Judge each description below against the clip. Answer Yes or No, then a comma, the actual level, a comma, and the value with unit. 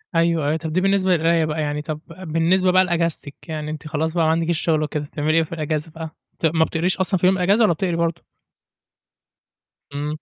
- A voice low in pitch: No, medium, 165 Hz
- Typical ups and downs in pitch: No, narrow, 1.9 semitones